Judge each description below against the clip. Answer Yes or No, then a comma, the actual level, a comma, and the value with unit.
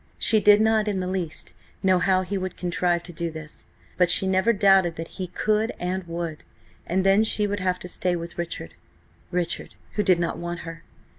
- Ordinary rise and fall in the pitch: No, narrow, 2.1 semitones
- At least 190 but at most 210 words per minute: Yes, average, 200 wpm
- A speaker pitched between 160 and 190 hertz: Yes, medium, 185 Hz